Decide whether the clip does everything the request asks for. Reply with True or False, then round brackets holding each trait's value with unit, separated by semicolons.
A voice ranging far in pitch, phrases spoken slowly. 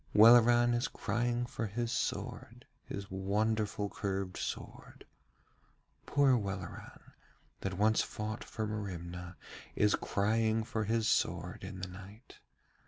False (2.9 semitones; 115 wpm)